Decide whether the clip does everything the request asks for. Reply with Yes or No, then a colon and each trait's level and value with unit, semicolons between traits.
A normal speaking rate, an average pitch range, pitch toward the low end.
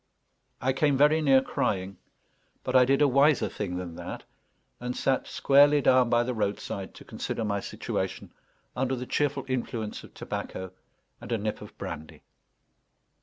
Yes: average, 160 wpm; average, 4.6 semitones; low, 125 Hz